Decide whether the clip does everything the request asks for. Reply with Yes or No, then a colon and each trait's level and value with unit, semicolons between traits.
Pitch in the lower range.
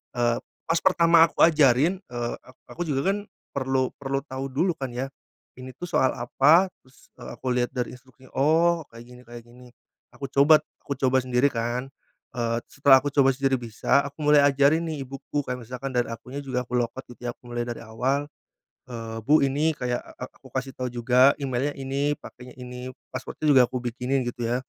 Yes: low, 130 Hz